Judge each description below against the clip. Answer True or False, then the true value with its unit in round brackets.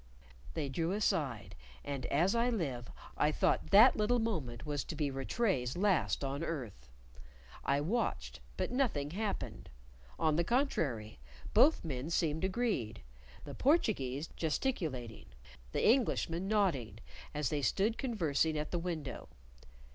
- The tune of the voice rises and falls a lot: True (7.5 semitones)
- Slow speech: True (130 wpm)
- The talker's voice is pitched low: False (160 Hz)